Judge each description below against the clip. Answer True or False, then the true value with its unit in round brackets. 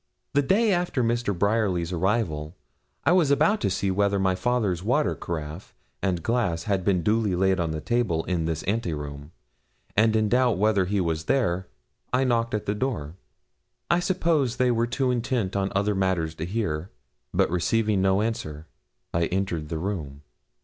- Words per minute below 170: False (175 wpm)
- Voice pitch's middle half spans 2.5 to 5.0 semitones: False (5.5 semitones)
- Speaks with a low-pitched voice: True (100 Hz)